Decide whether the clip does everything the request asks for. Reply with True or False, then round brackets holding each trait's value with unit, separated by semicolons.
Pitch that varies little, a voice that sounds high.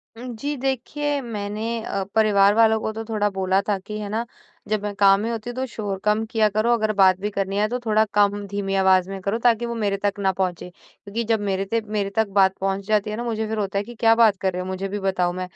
True (2.2 semitones; 210 Hz)